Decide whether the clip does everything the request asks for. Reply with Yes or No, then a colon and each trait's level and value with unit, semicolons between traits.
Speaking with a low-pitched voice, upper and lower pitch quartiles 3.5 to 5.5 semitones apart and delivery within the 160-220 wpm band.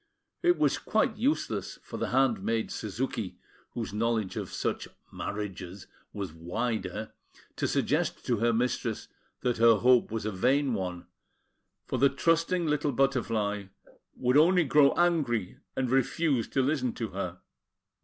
No: low, 120 Hz; average, 4.8 semitones; average, 140 wpm